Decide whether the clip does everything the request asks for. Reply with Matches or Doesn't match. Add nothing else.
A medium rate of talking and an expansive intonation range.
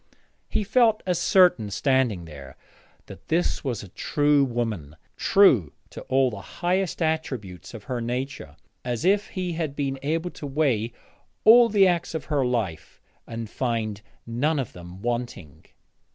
Matches